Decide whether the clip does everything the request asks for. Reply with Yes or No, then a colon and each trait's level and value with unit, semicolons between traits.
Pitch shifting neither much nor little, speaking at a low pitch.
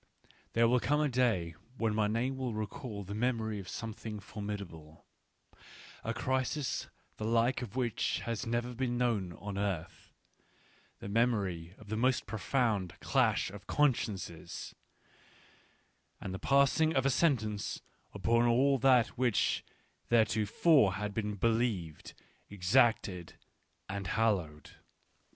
Yes: average, 3.7 semitones; low, 110 Hz